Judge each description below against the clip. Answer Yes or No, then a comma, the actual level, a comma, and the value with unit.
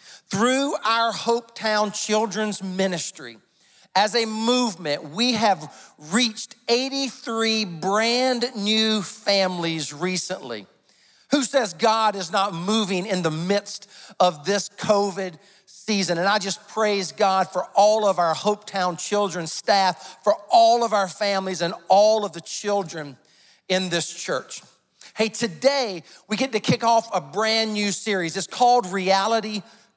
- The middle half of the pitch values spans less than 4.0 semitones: Yes, average, 3.2 semitones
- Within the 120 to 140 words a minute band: Yes, slow, 135 wpm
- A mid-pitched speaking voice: No, high, 205 Hz